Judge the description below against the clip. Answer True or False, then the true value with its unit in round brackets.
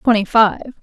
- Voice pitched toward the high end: True (220 Hz)